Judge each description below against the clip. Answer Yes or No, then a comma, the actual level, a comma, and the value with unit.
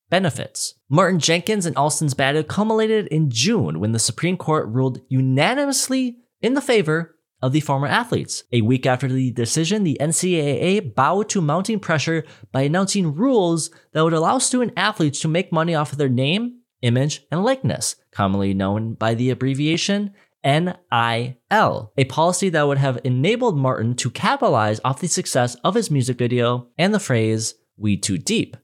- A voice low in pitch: No, medium, 155 Hz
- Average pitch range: No, wide, 6.3 semitones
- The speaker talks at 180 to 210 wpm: No, average, 165 wpm